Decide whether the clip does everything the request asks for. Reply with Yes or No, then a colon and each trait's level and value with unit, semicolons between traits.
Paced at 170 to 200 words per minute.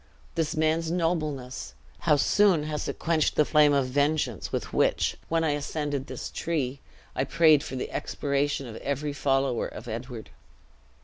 No: average, 160 wpm